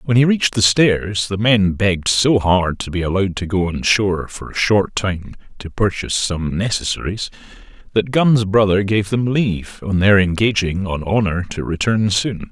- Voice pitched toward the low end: Yes, low, 100 Hz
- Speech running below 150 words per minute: No, average, 185 wpm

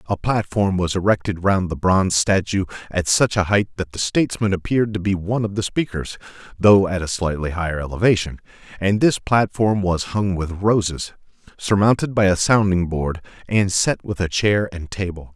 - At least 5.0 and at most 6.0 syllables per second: Yes, 5.2 syllables/s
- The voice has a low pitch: Yes, very low, 95 Hz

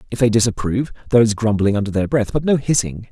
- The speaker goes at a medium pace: No, fast, 230 wpm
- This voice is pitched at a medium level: No, low, 115 Hz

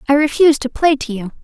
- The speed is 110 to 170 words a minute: No, fast, 250 wpm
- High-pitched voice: Yes, very high, 280 Hz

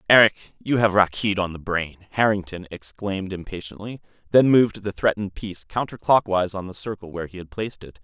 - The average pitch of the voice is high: No, low, 100 Hz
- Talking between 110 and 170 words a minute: No, average, 180 wpm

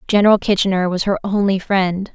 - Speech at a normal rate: Yes, average, 170 wpm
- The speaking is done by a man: No, female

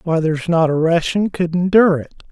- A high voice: No, medium, 170 Hz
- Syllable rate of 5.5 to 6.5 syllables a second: Yes, 5.8 syllables/s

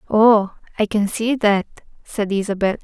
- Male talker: No, female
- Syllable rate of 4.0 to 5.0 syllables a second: Yes, 4.6 syllables/s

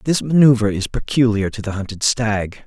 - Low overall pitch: Yes, low, 110 Hz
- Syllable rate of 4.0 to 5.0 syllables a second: No, 5.3 syllables/s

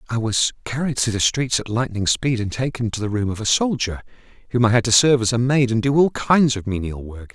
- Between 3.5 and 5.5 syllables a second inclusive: No, 5.8 syllables/s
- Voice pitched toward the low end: Yes, low, 120 Hz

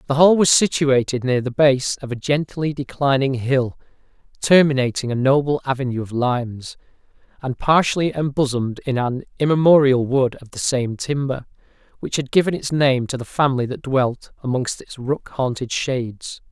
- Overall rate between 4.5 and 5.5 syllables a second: Yes, 5.0 syllables/s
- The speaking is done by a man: Yes, male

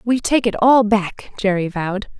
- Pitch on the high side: Yes, high, 210 Hz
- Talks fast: No, average, 190 wpm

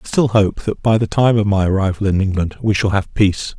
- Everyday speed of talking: No, fast, 270 wpm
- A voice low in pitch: Yes, low, 100 Hz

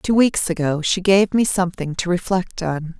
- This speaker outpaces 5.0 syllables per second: No, 4.8 syllables/s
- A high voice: No, medium, 180 Hz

